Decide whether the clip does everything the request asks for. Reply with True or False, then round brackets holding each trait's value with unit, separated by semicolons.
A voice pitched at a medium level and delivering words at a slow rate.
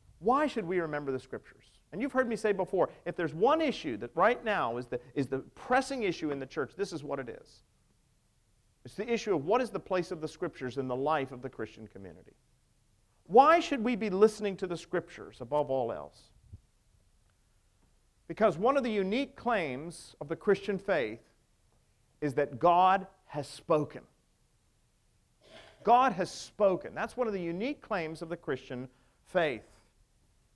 False (160 Hz; 175 wpm)